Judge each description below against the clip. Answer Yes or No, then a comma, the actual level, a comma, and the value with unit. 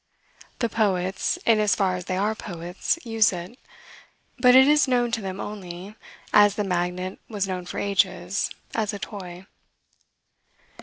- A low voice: No, high, 200 Hz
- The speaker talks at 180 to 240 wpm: No, average, 155 wpm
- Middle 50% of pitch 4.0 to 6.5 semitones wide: No, average, 3.1 semitones